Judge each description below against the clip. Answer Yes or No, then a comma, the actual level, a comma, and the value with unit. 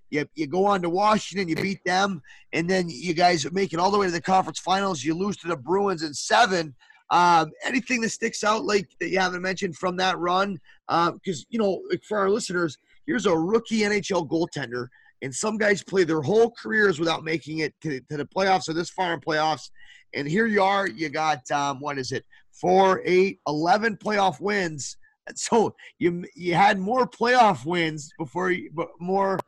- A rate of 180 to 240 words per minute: Yes, average, 200 wpm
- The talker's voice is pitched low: No, medium, 185 Hz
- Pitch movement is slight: No, average, 3.7 semitones